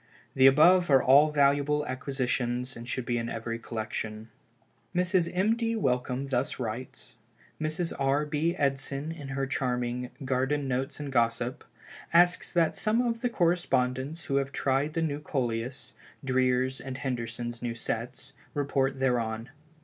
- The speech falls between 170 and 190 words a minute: No, average, 145 wpm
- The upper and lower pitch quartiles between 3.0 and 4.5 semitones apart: Yes, average, 3.3 semitones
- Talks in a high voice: No, low, 135 Hz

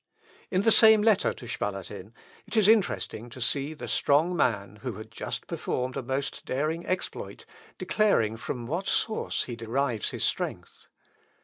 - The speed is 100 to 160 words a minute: Yes, average, 155 wpm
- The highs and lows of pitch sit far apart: Yes, wide, 8.0 semitones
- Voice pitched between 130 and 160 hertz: Yes, low, 135 Hz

